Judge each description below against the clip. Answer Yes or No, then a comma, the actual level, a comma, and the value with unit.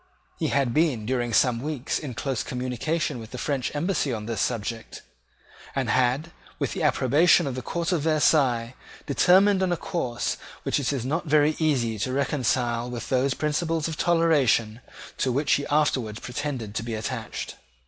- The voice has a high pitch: No, low, 135 Hz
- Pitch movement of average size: Yes, average, 4.3 semitones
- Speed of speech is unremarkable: Yes, average, 170 wpm